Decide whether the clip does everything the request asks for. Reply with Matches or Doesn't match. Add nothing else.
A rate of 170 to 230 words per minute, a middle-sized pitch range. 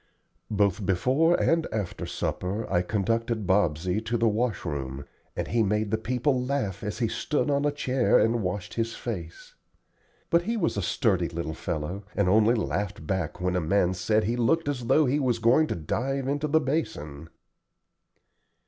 Doesn't match